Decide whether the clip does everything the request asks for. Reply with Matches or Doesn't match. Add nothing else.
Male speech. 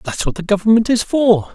Matches